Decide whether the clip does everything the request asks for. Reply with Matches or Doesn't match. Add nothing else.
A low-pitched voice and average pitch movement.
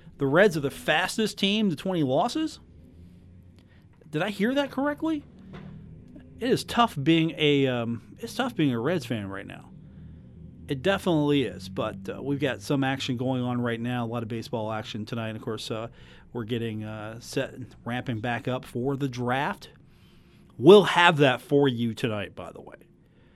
Doesn't match